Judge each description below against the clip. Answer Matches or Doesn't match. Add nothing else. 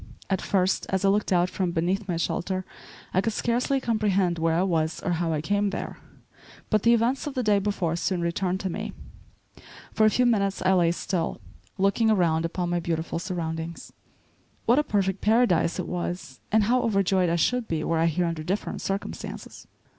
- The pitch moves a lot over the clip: Doesn't match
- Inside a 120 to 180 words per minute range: Doesn't match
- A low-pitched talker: Doesn't match